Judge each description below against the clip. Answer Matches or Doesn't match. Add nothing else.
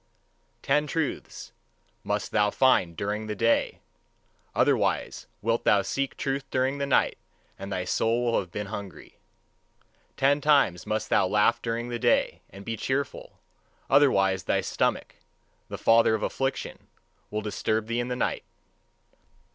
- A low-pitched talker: Matches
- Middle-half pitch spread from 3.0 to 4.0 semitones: Doesn't match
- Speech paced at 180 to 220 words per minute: Doesn't match